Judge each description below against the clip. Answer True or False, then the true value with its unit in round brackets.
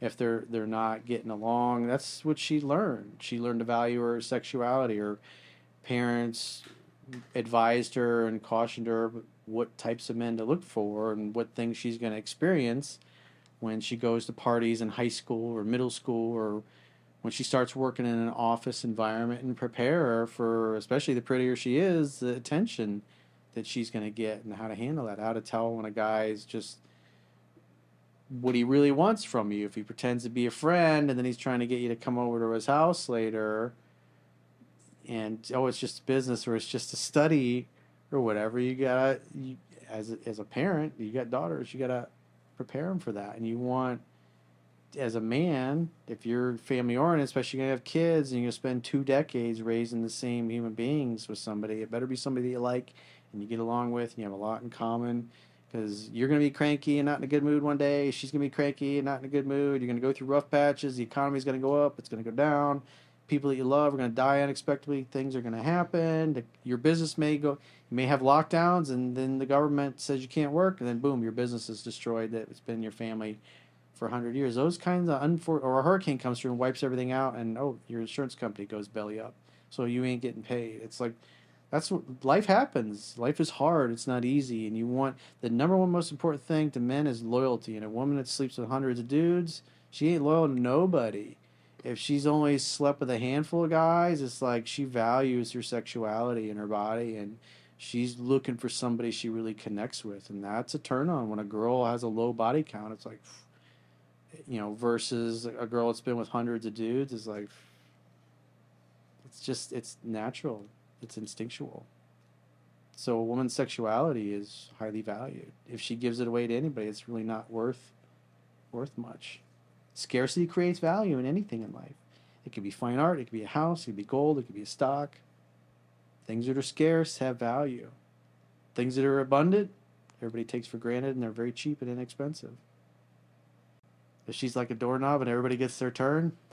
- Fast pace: True (210 wpm)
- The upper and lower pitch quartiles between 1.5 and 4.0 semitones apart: True (3.7 semitones)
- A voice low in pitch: True (120 Hz)